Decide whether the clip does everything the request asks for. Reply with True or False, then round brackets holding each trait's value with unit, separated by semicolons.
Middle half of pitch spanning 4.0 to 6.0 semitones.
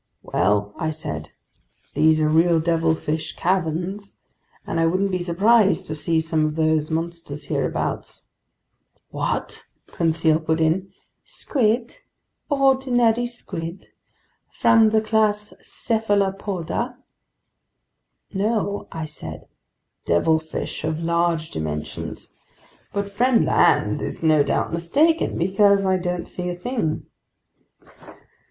True (4.7 semitones)